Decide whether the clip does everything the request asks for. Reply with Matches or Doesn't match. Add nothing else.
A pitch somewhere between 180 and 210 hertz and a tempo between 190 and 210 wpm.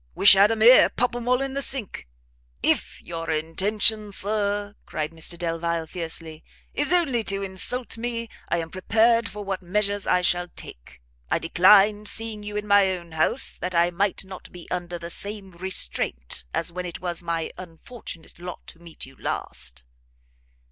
Doesn't match